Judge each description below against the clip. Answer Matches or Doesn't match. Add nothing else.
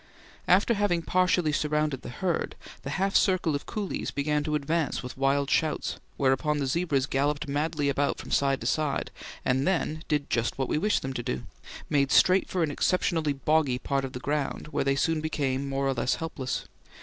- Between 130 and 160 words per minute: Doesn't match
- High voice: Doesn't match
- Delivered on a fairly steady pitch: Doesn't match